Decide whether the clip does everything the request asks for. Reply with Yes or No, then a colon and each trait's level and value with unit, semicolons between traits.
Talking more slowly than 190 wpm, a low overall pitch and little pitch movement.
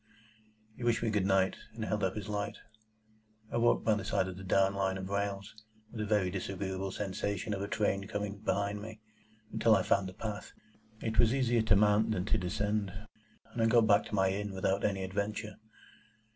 No: average, 200 wpm; low, 100 Hz; narrow, 2.0 semitones